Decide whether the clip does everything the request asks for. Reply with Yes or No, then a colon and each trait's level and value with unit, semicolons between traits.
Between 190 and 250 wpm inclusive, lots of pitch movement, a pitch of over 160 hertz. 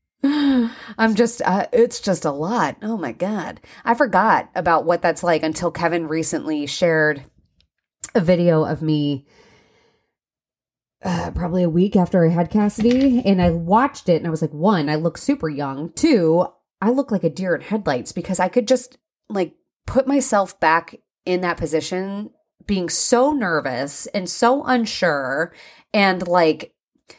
No: average, 160 wpm; wide, 6.1 semitones; medium, 185 Hz